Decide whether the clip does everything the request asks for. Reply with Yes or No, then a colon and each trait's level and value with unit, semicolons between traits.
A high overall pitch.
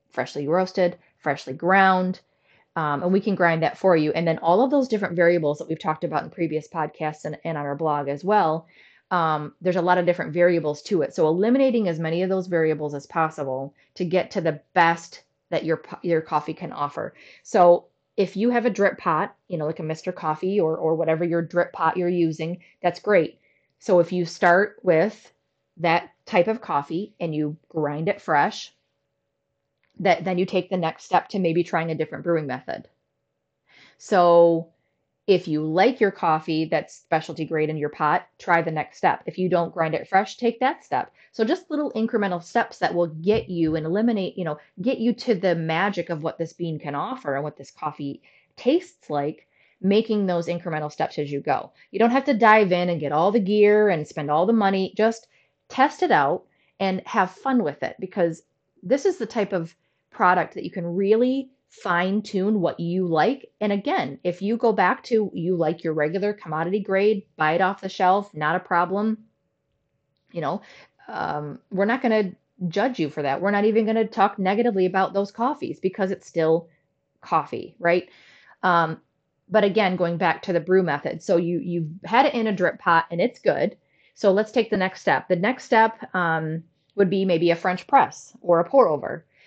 No: medium, 175 Hz